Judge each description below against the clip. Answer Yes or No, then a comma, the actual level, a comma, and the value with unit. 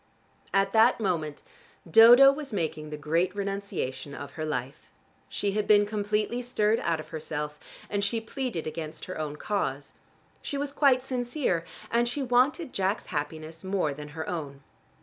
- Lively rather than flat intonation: Yes, wide, 7.1 semitones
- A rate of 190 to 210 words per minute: No, average, 160 wpm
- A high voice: Yes, high, 195 Hz